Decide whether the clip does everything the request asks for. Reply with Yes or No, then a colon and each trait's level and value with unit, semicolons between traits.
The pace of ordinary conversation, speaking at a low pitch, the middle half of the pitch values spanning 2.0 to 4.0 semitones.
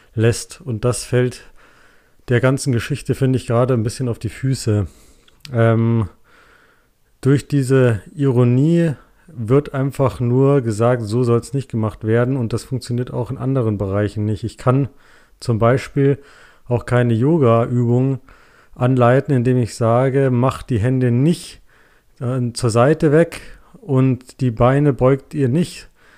Yes: average, 140 wpm; low, 125 Hz; narrow, 2.6 semitones